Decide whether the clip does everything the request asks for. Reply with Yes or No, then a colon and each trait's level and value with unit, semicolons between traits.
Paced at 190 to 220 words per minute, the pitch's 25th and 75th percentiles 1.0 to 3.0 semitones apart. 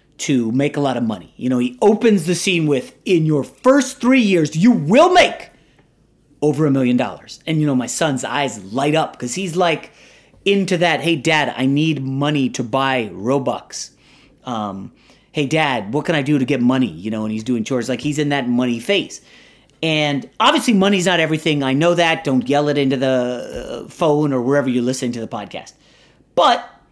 No: average, 200 wpm; average, 4.7 semitones